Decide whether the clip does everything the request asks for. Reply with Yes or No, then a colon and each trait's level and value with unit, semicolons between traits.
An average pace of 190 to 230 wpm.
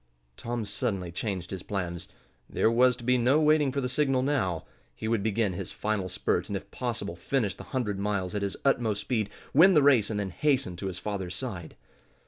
Yes: fast, 205 wpm